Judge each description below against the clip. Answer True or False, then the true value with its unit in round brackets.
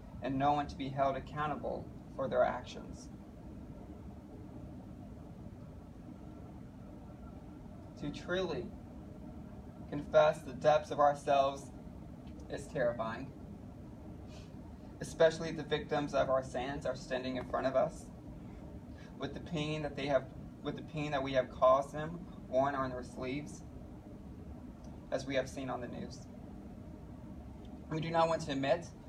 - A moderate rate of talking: False (125 wpm)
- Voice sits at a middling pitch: True (145 Hz)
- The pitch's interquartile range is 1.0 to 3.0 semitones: True (2.4 semitones)